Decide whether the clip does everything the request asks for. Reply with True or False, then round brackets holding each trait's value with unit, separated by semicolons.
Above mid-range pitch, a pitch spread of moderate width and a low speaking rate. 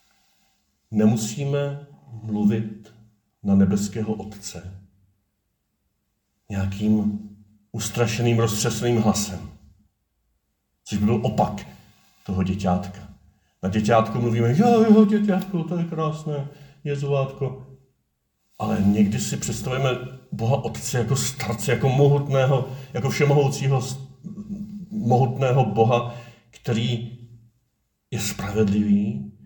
False (115 Hz; 4.7 semitones; 90 wpm)